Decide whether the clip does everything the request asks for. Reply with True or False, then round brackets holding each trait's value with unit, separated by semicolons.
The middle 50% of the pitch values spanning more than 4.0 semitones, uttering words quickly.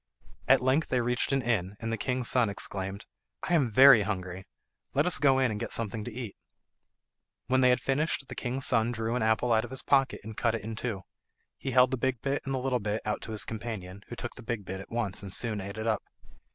False (3.4 semitones; 245 wpm)